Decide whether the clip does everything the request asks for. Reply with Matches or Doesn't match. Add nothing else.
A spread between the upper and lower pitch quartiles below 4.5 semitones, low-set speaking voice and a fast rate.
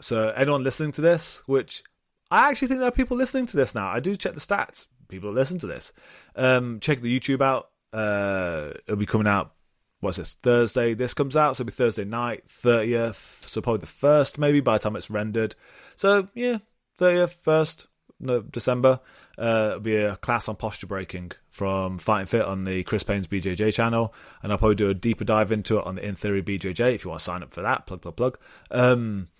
Doesn't match